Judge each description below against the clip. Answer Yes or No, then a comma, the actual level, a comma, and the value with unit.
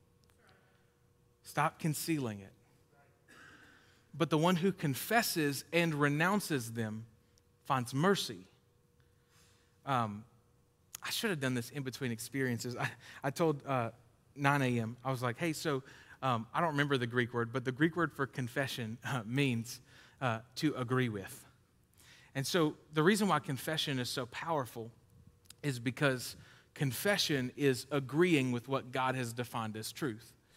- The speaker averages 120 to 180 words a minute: Yes, average, 145 wpm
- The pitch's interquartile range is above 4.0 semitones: No, average, 3.4 semitones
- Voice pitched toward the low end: Yes, low, 130 Hz